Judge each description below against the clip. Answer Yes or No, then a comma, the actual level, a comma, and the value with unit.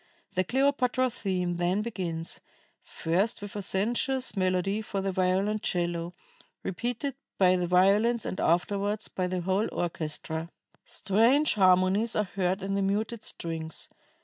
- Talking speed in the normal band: No, slow, 130 wpm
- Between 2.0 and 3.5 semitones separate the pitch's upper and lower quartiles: Yes, average, 3.1 semitones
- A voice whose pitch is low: No, high, 195 Hz